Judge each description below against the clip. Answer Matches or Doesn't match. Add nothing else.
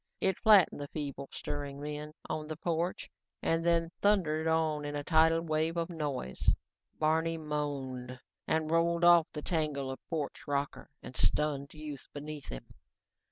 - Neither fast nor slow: Matches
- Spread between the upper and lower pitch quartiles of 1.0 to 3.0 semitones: Matches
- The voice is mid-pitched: Matches